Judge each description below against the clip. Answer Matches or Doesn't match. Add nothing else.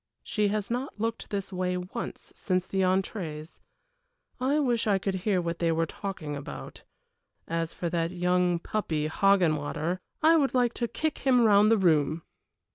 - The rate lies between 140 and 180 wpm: Matches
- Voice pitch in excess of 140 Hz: Matches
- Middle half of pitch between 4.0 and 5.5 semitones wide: Matches